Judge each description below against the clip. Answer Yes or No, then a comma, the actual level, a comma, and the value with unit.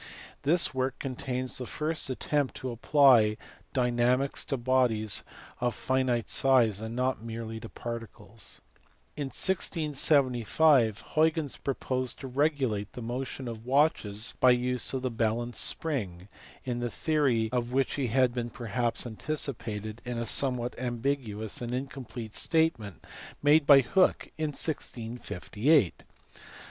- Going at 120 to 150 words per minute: Yes, slow, 135 wpm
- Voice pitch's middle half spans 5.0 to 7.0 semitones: No, average, 3.2 semitones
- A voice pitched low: Yes, low, 125 Hz